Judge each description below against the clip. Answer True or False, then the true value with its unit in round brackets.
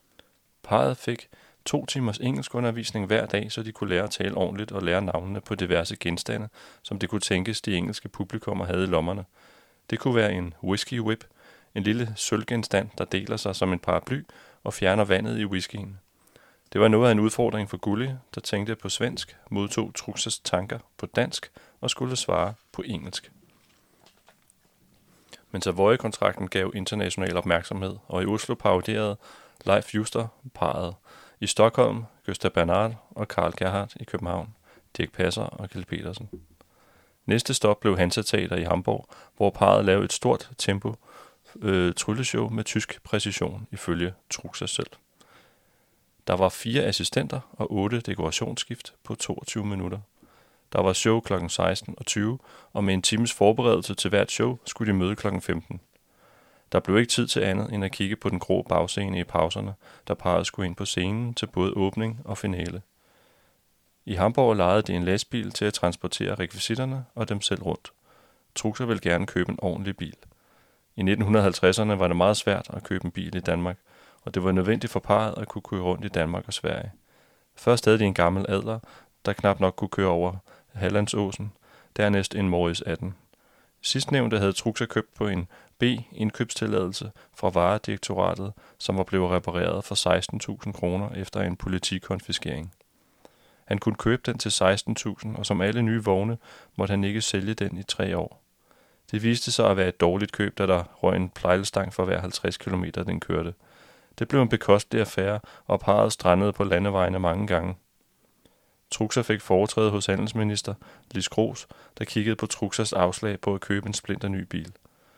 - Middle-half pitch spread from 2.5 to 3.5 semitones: True (2.9 semitones)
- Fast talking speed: False (170 wpm)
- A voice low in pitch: True (100 Hz)